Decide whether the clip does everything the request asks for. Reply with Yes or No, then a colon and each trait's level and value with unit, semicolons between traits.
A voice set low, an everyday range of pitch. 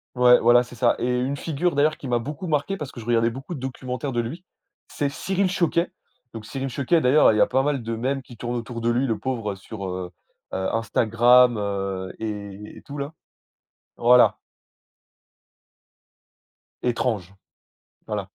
Yes: low, 125 Hz; average, 3.7 semitones